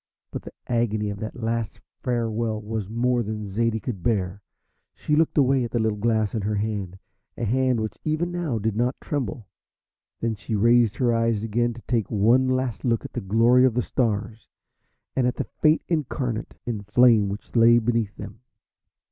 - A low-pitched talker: Yes, low, 115 Hz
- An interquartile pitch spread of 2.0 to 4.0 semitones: Yes, narrow, 2.5 semitones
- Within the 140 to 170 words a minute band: No, average, 185 wpm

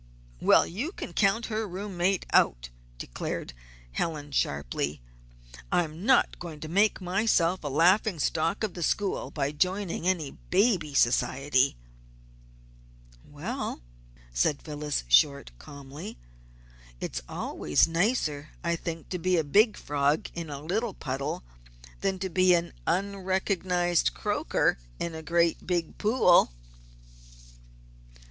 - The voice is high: No, medium, 170 Hz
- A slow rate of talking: Yes, slow, 125 wpm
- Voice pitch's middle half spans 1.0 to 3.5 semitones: No, average, 4.5 semitones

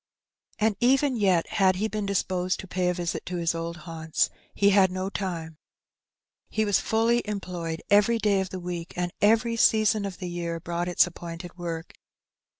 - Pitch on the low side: No, medium, 185 Hz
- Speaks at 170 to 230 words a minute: Yes, average, 180 wpm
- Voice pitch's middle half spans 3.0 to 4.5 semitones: Yes, average, 3.3 semitones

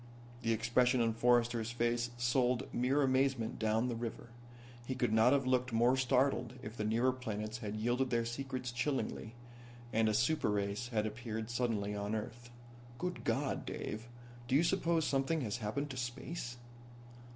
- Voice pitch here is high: No, low, 120 Hz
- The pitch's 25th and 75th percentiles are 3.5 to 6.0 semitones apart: No, narrow, 2.5 semitones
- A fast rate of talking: No, average, 160 wpm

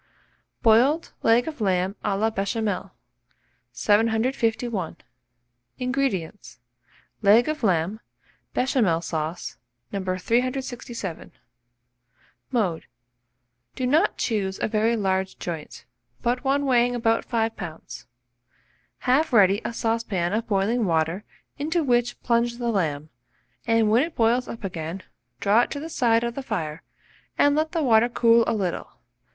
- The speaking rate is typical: No, slow, 130 wpm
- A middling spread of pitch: Yes, average, 4.4 semitones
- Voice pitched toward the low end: No, high, 225 Hz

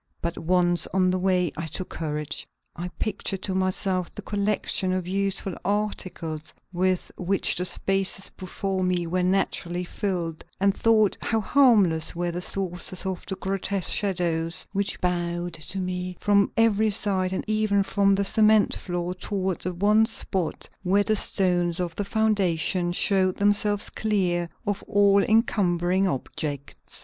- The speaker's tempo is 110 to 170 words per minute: Yes, average, 150 wpm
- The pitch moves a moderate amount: No, narrow, 2.3 semitones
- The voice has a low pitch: No, medium, 185 Hz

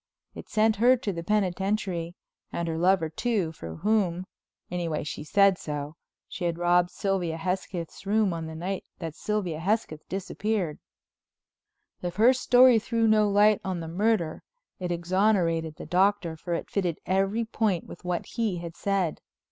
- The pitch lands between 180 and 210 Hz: Yes, medium, 185 Hz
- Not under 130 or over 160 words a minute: Yes, average, 155 wpm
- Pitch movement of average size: Yes, average, 3.9 semitones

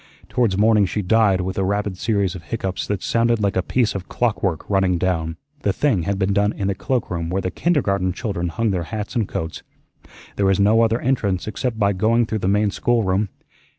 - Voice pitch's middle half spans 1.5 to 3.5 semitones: Yes, average, 3.0 semitones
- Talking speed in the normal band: No, fast, 210 wpm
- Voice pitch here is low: Yes, low, 100 Hz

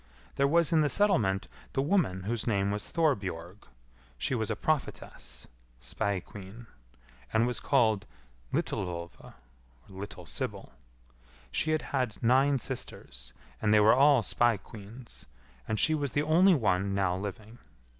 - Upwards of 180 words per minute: No, average, 140 wpm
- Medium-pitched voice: No, low, 110 Hz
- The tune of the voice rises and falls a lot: Yes, wide, 6.1 semitones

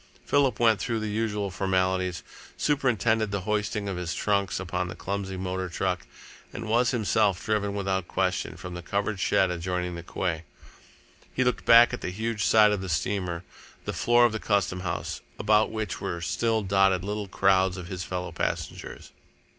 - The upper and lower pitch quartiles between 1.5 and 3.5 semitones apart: Yes, average, 3.0 semitones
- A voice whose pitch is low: Yes, low, 100 Hz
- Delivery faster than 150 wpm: Yes, average, 175 wpm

